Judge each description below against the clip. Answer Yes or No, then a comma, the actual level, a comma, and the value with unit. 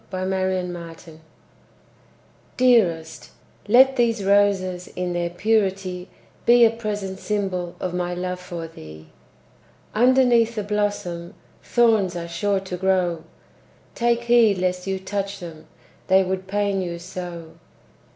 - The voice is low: No, high, 190 Hz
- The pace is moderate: No, slow, 130 wpm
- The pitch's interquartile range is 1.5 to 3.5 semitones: Yes, average, 2.8 semitones